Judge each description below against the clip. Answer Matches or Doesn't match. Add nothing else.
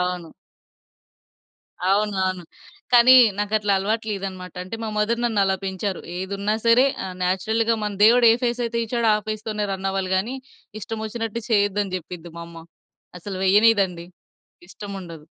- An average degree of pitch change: Matches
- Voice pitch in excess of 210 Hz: Doesn't match